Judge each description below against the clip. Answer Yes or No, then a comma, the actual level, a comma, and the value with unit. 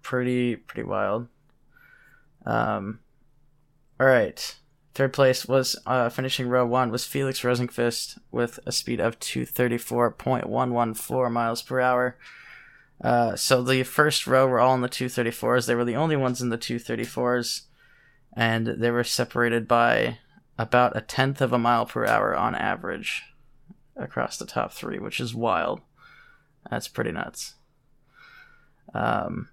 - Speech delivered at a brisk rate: No, average, 140 wpm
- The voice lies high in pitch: No, low, 125 Hz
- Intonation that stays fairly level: Yes, narrow, 1.9 semitones